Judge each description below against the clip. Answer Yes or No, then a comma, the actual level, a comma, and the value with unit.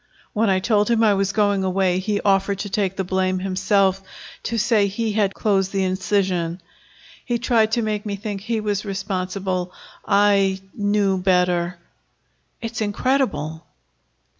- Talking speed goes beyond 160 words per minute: No, average, 150 wpm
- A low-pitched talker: No, high, 195 Hz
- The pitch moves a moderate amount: No, narrow, 2.0 semitones